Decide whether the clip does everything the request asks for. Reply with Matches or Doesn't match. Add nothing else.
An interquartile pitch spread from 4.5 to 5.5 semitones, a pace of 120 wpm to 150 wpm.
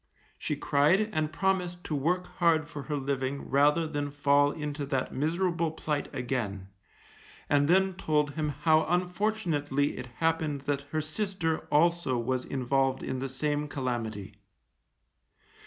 Doesn't match